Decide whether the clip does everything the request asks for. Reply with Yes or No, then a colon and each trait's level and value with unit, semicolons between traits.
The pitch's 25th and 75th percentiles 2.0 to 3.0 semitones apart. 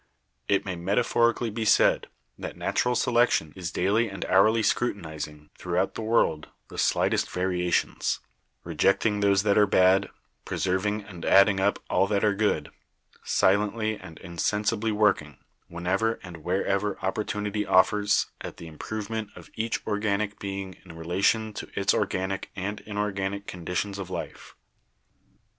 Yes: narrow, 2.4 semitones